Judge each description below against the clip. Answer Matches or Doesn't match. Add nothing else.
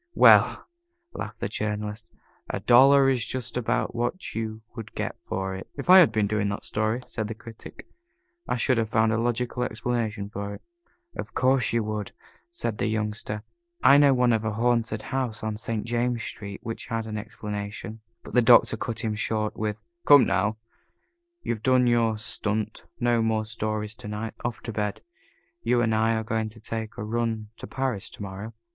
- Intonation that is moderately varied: Doesn't match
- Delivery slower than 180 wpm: Doesn't match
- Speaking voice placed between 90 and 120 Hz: Matches